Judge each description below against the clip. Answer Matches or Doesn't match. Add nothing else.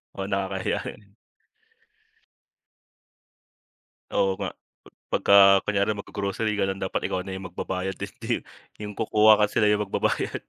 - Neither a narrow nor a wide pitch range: Doesn't match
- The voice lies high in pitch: Doesn't match